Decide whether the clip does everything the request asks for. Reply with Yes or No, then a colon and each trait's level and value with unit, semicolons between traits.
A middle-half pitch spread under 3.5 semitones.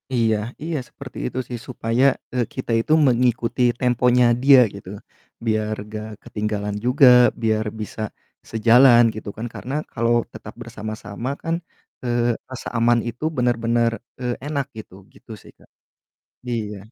Yes: narrow, 2.4 semitones